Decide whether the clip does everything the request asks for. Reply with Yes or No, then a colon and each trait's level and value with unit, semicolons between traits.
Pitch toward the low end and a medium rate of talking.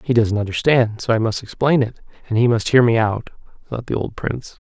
No: low, 115 Hz; fast, 230 wpm